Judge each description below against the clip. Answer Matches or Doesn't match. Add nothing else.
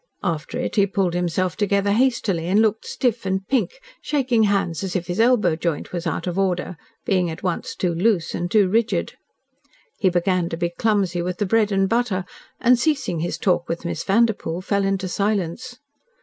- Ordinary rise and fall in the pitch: Matches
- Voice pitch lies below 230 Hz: Matches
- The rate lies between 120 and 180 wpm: Doesn't match